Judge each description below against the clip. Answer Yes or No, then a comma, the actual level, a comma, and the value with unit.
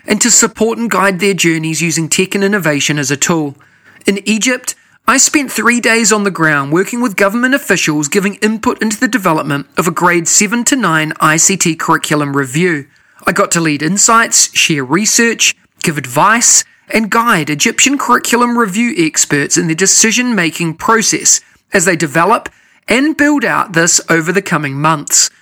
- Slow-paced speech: No, average, 170 wpm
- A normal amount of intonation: No, wide, 6.1 semitones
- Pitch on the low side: No, high, 200 Hz